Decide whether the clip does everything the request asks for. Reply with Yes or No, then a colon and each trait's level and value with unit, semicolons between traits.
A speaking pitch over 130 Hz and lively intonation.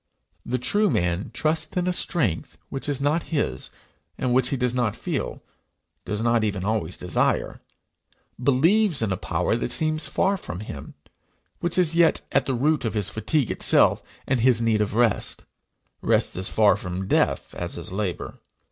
No: low, 120 Hz; wide, 7.2 semitones